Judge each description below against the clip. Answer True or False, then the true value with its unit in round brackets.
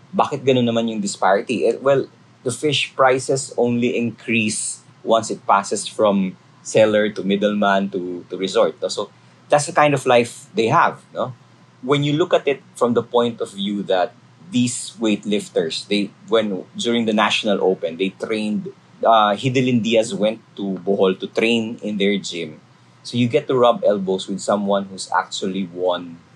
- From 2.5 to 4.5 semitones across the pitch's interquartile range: True (4.0 semitones)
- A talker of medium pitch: False (110 Hz)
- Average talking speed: False (170 wpm)